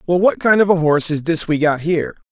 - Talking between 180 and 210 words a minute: No, fast, 285 wpm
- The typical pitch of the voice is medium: Yes, medium, 165 Hz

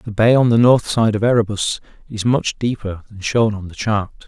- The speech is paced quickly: Yes, fast, 225 wpm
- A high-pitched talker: No, low, 110 Hz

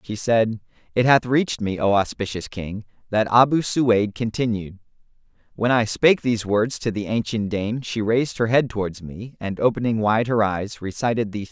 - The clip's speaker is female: No, male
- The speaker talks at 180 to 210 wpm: Yes, average, 195 wpm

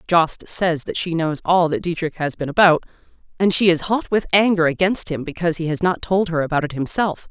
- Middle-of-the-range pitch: Yes, medium, 170 Hz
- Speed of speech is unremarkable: No, fast, 230 wpm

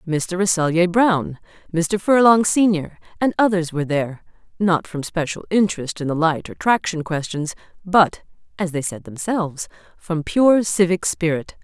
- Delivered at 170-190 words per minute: No, average, 150 wpm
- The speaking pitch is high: No, medium, 175 Hz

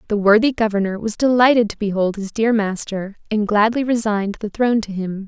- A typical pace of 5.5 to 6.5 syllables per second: Yes, 5.7 syllables/s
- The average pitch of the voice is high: Yes, high, 215 Hz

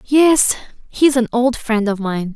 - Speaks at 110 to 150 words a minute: No, fast, 205 wpm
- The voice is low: No, high, 240 Hz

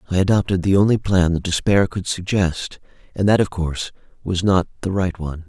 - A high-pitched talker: No, very low, 90 Hz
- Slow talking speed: No, average, 195 wpm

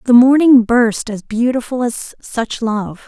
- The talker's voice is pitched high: Yes, high, 235 Hz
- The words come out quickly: No, average, 155 wpm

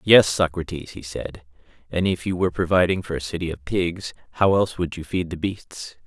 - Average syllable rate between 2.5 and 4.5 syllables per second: No, 5.4 syllables/s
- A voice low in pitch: Yes, very low, 85 Hz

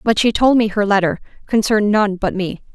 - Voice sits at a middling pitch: No, high, 205 Hz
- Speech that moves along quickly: Yes, fast, 220 wpm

